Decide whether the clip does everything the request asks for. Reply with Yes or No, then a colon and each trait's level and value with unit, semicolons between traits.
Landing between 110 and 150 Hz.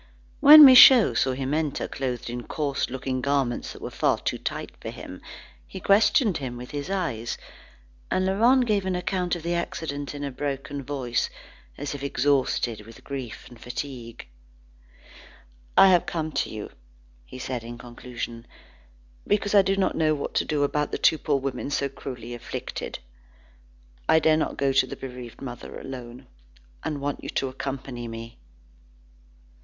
Yes: medium, 140 Hz